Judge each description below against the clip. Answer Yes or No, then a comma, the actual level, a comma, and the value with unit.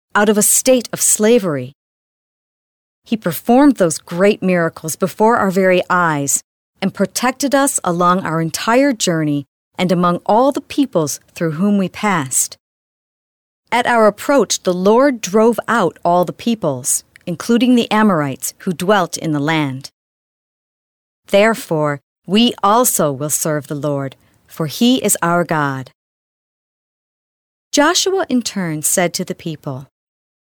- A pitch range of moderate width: No, wide, 5.9 semitones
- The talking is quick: No, slow, 135 wpm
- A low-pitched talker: No, medium, 185 Hz